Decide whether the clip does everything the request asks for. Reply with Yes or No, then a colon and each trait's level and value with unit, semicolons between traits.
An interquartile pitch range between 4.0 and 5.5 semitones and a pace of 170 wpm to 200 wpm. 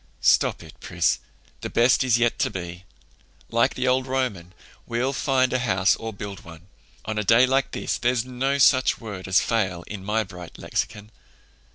Yes: average, 5.1 semitones; average, 180 wpm